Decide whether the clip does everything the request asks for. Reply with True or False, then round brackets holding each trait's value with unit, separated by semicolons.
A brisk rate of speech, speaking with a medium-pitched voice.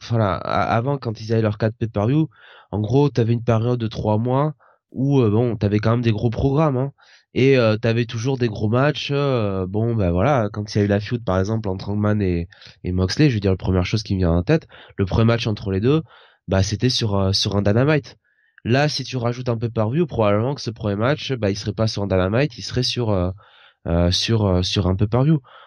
False (250 wpm; 115 Hz)